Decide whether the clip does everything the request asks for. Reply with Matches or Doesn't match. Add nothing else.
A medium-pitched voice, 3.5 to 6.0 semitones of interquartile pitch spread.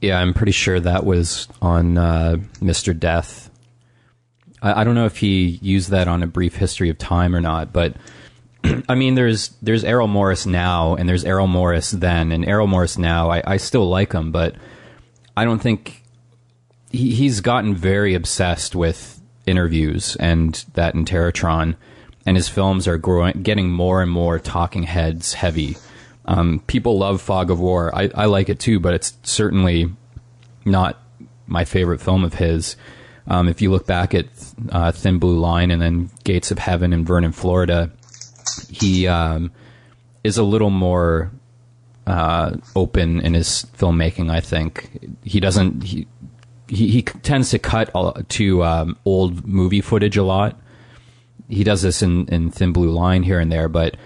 Doesn't match